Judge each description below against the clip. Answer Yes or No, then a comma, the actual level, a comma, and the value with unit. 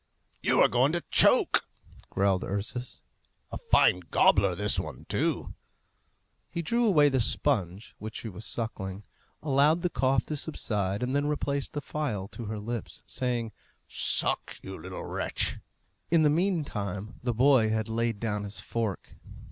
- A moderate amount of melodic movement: No, wide, 5.8 semitones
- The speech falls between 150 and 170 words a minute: Yes, average, 155 wpm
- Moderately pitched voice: No, low, 115 Hz